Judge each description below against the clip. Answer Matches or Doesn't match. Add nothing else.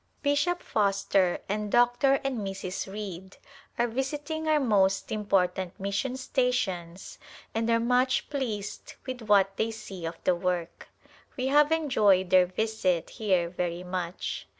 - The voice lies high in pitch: Matches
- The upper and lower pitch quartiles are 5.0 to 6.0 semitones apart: Matches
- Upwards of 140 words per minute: Doesn't match